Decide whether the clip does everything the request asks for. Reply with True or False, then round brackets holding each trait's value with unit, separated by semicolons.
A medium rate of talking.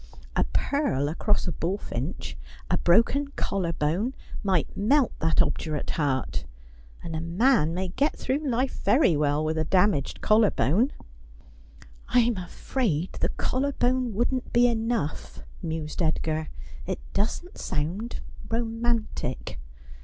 False (130 wpm)